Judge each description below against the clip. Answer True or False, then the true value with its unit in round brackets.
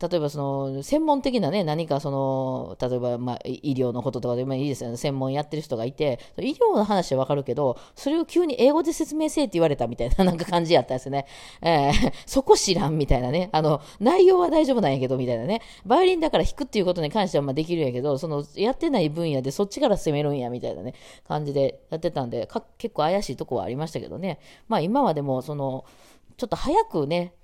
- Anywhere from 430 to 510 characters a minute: True (455 characters per minute)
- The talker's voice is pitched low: False (155 Hz)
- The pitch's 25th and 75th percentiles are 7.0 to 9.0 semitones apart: True (8.5 semitones)